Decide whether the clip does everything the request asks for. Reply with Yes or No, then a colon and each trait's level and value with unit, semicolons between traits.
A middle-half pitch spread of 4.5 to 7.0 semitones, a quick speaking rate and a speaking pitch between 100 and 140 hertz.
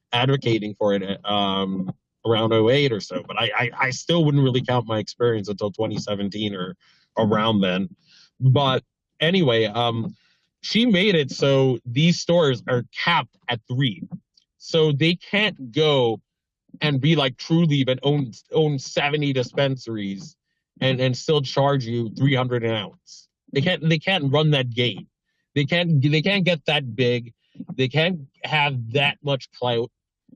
No: average, 4.9 semitones; average, 155 wpm; low, 135 Hz